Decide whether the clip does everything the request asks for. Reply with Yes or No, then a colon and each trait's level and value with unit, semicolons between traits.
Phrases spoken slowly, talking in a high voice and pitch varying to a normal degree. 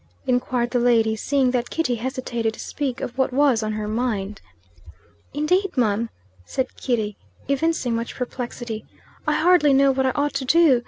No: average, 165 wpm; very high, 250 Hz; average, 3.2 semitones